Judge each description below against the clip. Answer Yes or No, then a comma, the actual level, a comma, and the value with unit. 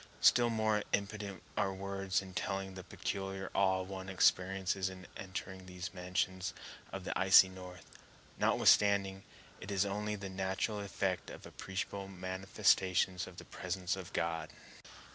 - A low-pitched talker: Yes, very low, 95 Hz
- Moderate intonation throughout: No, narrow, 1.0 semitones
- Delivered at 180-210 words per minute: No, average, 140 wpm